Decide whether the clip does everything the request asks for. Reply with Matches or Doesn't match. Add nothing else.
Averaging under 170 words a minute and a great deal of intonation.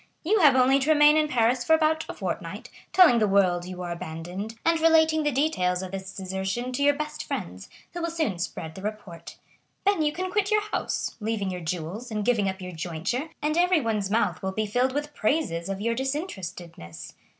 Doesn't match